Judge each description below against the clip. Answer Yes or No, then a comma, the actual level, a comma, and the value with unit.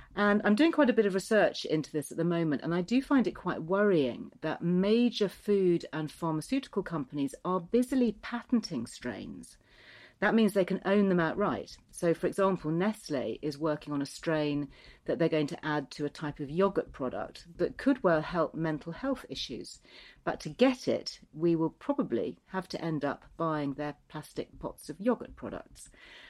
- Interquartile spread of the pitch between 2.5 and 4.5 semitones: No, average, 5.1 semitones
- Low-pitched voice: No, medium, 170 Hz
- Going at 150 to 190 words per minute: Yes, average, 185 wpm